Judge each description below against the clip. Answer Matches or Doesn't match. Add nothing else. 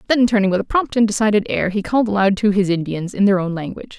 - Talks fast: Matches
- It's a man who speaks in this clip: Doesn't match